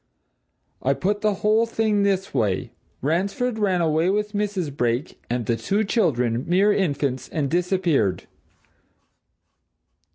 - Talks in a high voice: No, medium, 180 Hz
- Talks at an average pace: No, slow, 125 wpm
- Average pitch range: No, wide, 7.0 semitones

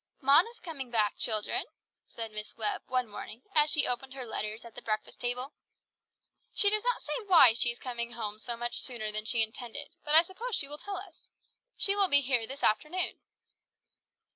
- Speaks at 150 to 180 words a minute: No, average, 195 wpm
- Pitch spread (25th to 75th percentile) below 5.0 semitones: No, wide, 5.4 semitones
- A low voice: No, very high, 250 Hz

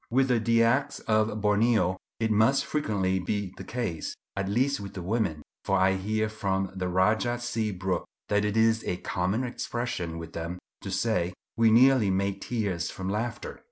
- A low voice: Yes, low, 105 Hz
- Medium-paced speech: Yes, average, 175 wpm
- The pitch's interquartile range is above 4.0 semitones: No, average, 3.5 semitones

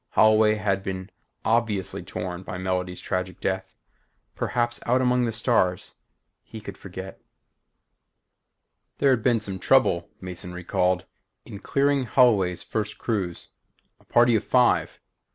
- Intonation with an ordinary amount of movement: Yes, average, 4.4 semitones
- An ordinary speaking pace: No, slow, 130 wpm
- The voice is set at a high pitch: No, low, 100 Hz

